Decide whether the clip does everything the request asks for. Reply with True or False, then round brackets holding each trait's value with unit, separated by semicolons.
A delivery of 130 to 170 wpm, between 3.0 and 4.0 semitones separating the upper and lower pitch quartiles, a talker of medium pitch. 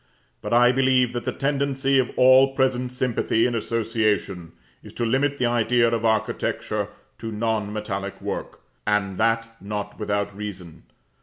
False (150 wpm; 3.4 semitones; 115 Hz)